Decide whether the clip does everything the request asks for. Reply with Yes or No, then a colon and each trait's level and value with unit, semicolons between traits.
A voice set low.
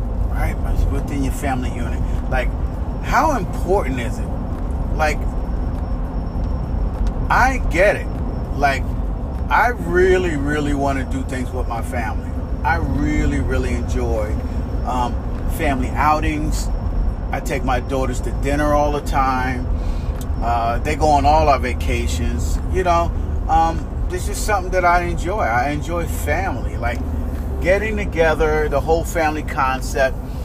Yes: very low, 80 Hz